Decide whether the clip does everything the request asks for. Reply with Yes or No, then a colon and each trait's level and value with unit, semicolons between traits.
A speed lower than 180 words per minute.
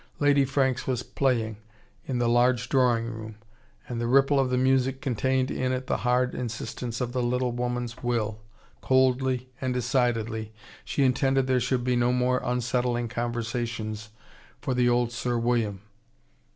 Yes: average, 155 wpm